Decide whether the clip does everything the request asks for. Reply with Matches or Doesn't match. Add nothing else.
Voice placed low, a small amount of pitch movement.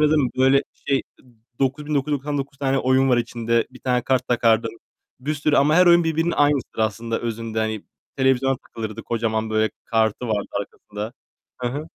Doesn't match